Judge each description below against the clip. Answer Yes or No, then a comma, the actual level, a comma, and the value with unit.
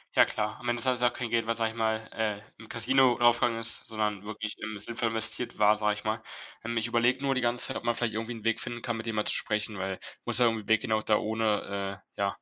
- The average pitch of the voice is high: No, low, 110 Hz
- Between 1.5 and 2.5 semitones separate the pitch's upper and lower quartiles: Yes, narrow, 1.8 semitones